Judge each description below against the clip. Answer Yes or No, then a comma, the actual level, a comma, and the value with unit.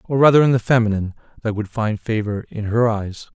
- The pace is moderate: No, fast, 215 wpm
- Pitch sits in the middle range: No, low, 115 Hz